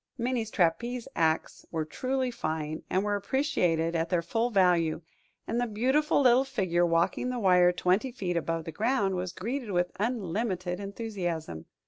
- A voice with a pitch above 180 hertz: Yes, high, 190 Hz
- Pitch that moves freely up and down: Yes, wide, 6.0 semitones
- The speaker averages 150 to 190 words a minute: Yes, average, 155 wpm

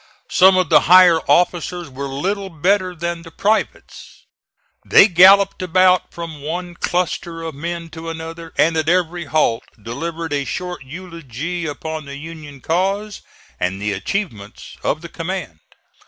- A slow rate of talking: No, average, 145 wpm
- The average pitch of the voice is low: No, medium, 165 Hz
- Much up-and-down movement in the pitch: No, average, 3.0 semitones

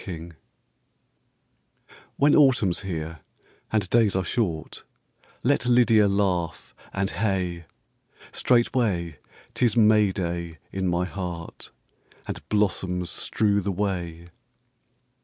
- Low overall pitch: Yes, very low, 95 Hz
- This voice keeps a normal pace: No, slow, 100 wpm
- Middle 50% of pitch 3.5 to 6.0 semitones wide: Yes, average, 3.9 semitones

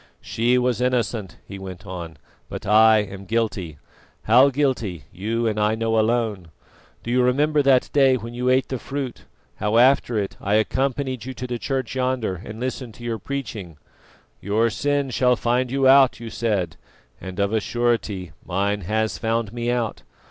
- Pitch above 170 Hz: No, low, 115 Hz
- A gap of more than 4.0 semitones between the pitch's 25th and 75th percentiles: No, average, 3.5 semitones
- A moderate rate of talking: Yes, average, 175 wpm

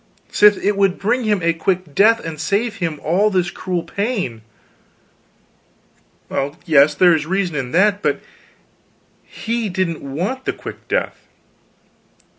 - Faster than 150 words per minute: No, average, 140 wpm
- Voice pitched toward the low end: No, medium, 185 Hz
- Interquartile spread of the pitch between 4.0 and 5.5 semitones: Yes, average, 4.3 semitones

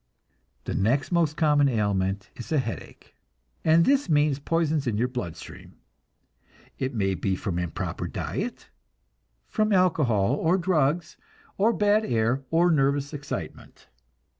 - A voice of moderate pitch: Yes, medium, 145 Hz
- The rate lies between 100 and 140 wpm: Yes, slow, 135 wpm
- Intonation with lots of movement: Yes, wide, 6.5 semitones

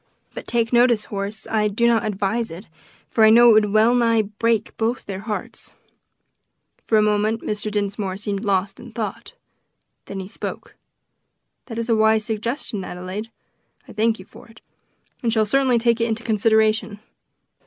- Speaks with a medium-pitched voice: No, high, 220 Hz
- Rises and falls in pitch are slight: Yes, narrow, 2.0 semitones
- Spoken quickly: No, average, 165 wpm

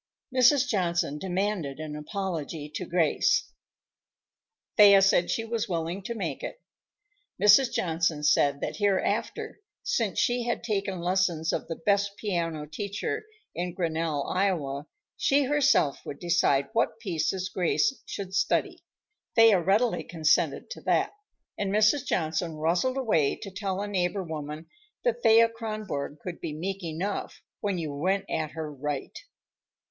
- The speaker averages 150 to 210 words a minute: No, average, 140 wpm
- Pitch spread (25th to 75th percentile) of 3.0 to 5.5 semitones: Yes, average, 4.7 semitones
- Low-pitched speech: No, medium, 185 Hz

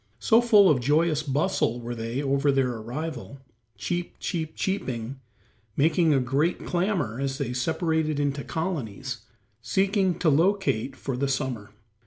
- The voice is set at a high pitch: No, medium, 140 Hz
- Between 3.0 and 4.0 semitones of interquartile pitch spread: No, average, 5.0 semitones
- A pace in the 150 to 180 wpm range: No, average, 140 wpm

